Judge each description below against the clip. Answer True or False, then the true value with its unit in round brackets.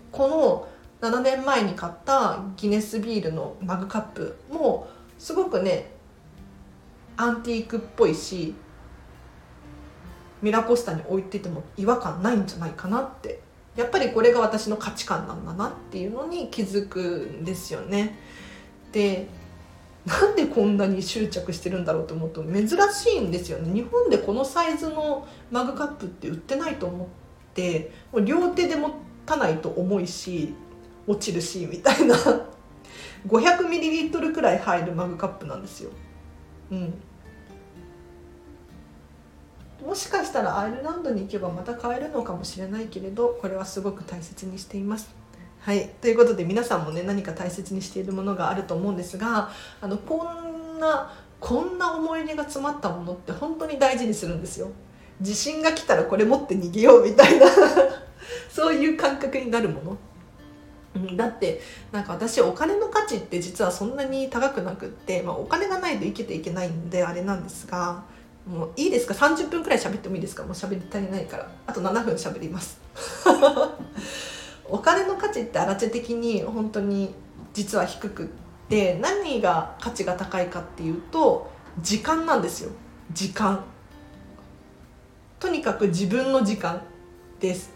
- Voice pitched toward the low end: False (205 Hz)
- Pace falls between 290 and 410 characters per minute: True (320 characters per minute)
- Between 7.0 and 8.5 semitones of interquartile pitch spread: True (7.4 semitones)